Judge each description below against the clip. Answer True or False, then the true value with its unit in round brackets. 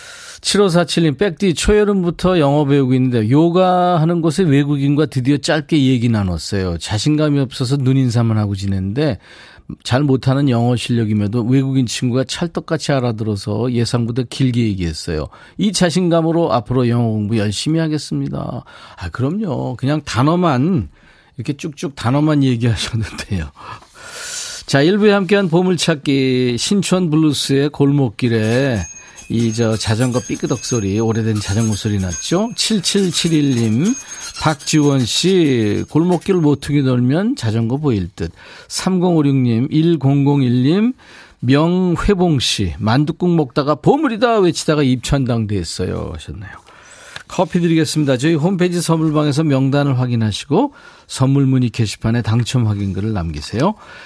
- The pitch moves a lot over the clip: True (6.2 semitones)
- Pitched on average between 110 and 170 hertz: True (140 Hz)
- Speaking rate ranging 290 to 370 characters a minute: True (300 characters per minute)